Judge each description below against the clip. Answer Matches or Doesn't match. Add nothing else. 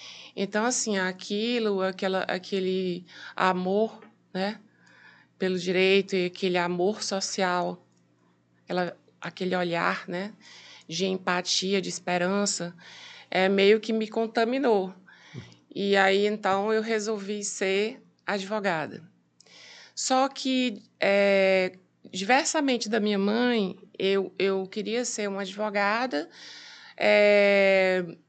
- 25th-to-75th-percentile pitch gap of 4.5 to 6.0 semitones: Doesn't match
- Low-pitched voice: Doesn't match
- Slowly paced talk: Matches